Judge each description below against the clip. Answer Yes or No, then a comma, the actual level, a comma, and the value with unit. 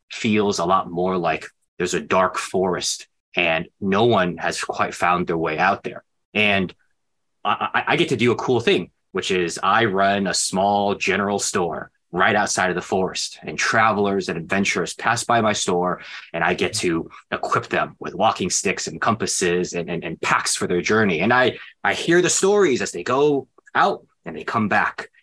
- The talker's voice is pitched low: Yes, low, 100 Hz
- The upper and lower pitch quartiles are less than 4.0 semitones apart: Yes, average, 3.3 semitones